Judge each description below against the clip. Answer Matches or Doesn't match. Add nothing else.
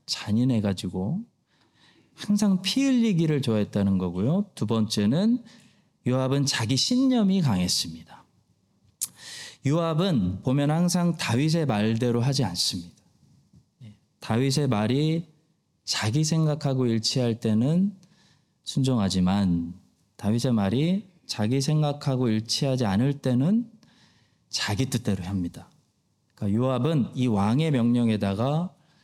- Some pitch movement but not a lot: Doesn't match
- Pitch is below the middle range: Matches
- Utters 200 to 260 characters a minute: Matches